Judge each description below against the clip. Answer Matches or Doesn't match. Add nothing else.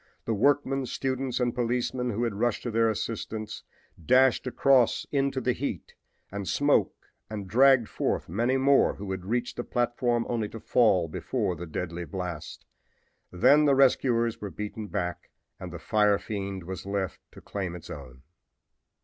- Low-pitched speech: Matches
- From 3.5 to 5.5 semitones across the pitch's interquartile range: Matches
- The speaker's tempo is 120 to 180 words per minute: Matches